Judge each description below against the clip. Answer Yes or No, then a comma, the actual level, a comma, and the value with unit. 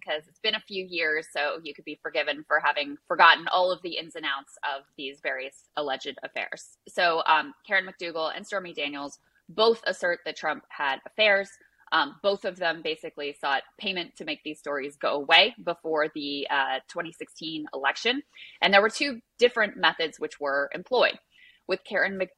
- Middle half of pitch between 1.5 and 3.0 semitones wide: No, average, 5.0 semitones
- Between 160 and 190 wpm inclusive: Yes, average, 180 wpm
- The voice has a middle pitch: Yes, medium, 170 Hz